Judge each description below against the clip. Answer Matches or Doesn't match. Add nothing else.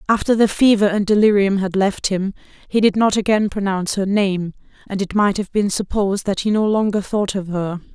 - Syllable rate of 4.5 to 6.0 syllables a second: Matches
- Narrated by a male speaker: Doesn't match